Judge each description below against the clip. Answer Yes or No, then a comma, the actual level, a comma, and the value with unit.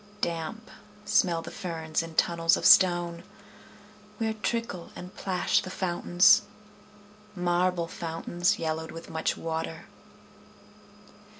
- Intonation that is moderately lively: No, narrow, 1.9 semitones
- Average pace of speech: No, slow, 105 wpm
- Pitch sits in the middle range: Yes, medium, 175 Hz